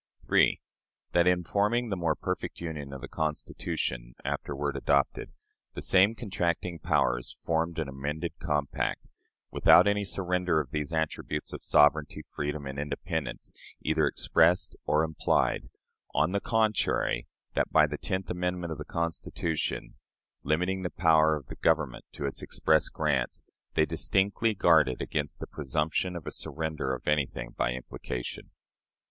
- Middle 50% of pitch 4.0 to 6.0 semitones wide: No, average, 3.5 semitones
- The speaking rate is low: No, average, 145 wpm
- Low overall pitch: Yes, very low, 80 Hz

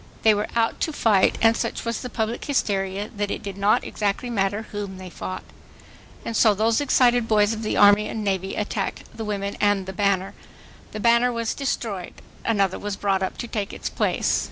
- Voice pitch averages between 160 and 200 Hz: No, high, 210 Hz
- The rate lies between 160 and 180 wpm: No, average, 200 wpm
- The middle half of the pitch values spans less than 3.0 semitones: Yes, narrow, 2.4 semitones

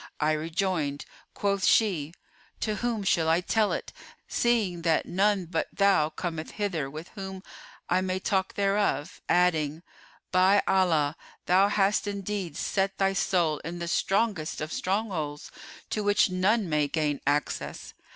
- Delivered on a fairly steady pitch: No, average, 4.0 semitones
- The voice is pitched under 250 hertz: Yes, medium, 185 Hz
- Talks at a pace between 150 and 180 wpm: No, average, 140 wpm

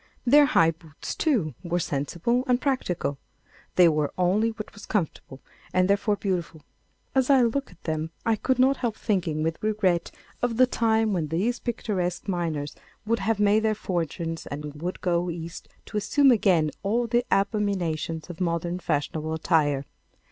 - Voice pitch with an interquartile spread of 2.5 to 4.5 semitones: No, wide, 5.4 semitones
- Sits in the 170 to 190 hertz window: Yes, medium, 185 Hz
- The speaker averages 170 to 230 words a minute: No, average, 160 wpm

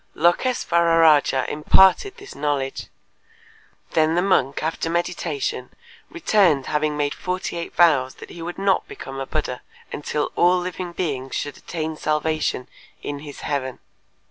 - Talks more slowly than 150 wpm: Yes, slow, 135 wpm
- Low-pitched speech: No, medium, 155 Hz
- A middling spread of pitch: Yes, average, 3.4 semitones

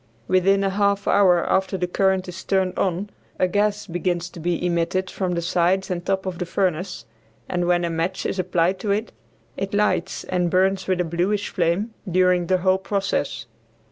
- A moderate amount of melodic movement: No, narrow, 1.7 semitones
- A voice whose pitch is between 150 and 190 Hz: Yes, medium, 185 Hz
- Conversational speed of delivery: Yes, average, 190 wpm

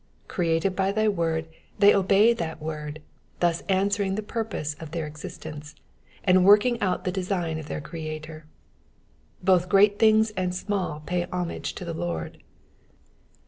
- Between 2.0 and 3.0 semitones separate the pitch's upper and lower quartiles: No, average, 3.9 semitones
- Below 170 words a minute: Yes, average, 150 wpm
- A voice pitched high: No, medium, 180 Hz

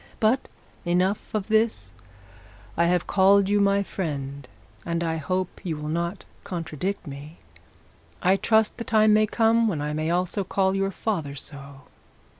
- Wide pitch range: No, average, 4.5 semitones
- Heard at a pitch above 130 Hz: Yes, medium, 185 Hz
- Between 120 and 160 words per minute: Yes, average, 155 wpm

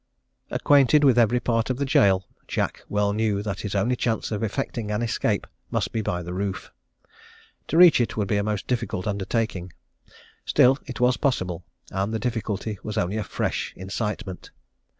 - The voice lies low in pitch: Yes, low, 105 Hz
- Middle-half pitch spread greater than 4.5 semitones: No, average, 3.7 semitones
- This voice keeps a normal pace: Yes, average, 175 wpm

